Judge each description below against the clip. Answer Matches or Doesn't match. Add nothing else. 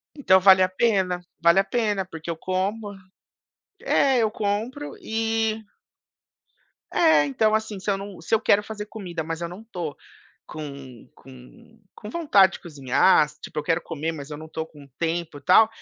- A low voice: Doesn't match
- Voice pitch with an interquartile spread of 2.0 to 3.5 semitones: Doesn't match